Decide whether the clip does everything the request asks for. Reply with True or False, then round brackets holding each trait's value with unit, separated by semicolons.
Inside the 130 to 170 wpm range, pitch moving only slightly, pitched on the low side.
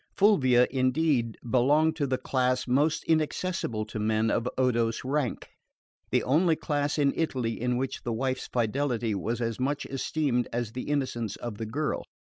False (160 wpm; 3.7 semitones; 130 Hz)